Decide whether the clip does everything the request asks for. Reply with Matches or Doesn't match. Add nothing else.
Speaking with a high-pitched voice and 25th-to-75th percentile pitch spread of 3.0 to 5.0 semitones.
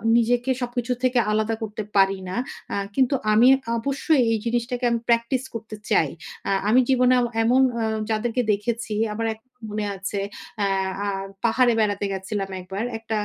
Doesn't match